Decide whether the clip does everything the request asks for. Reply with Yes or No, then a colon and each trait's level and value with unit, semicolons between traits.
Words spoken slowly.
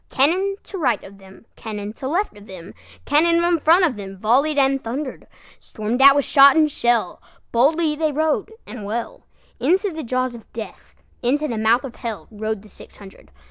No: average, 155 wpm